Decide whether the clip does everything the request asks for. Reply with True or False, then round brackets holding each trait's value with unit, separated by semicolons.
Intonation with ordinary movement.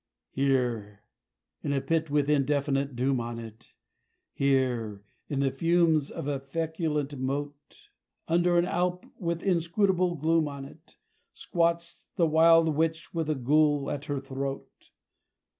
True (3.3 semitones)